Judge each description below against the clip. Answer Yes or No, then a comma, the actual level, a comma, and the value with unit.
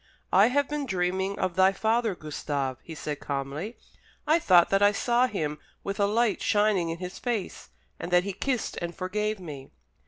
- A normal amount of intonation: Yes, average, 4.2 semitones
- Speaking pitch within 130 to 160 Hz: No, high, 190 Hz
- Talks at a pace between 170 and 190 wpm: Yes, average, 185 wpm